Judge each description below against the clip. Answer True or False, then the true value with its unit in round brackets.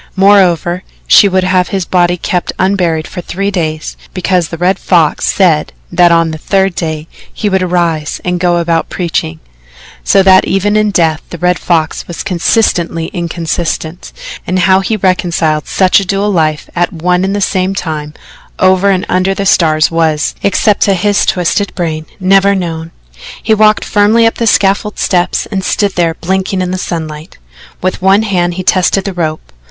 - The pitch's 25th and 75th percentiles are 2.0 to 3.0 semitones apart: True (2.6 semitones)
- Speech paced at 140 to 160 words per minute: False (175 wpm)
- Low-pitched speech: False (180 Hz)